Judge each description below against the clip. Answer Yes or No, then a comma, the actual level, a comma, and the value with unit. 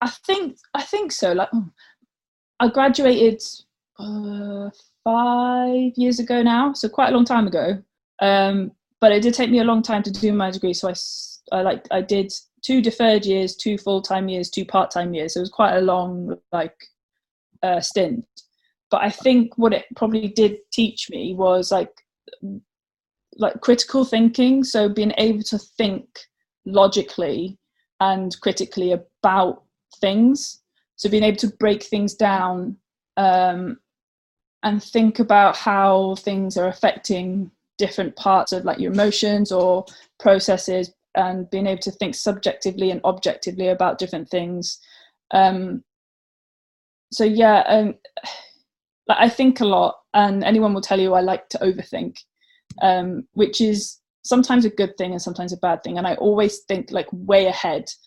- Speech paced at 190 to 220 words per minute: No, average, 155 wpm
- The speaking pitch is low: No, high, 205 Hz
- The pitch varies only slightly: No, average, 3.5 semitones